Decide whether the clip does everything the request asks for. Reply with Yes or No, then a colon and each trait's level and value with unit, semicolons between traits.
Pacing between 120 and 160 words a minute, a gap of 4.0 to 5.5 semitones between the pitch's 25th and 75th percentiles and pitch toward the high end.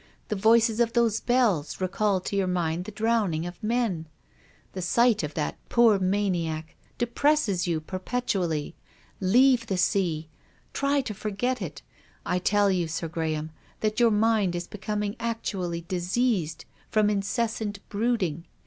Yes: average, 140 wpm; average, 4.6 semitones; high, 200 Hz